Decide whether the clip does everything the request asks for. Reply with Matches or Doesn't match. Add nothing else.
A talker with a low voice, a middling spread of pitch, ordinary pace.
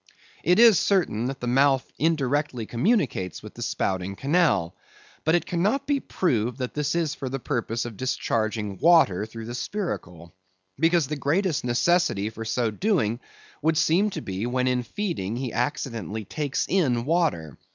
Doesn't match